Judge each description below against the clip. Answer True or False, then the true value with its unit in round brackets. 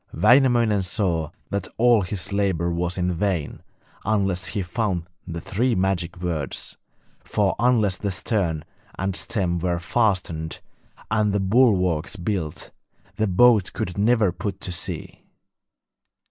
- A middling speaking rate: False (130 wpm)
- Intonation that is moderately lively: True (3.5 semitones)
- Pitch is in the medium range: False (95 Hz)